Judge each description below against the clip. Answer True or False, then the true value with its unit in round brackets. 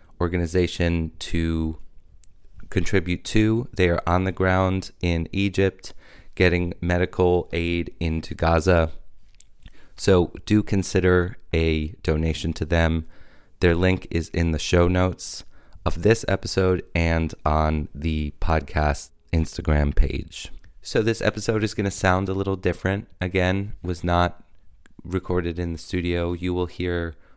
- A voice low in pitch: True (90 Hz)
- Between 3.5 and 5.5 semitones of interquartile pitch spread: False (2.4 semitones)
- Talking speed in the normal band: False (130 wpm)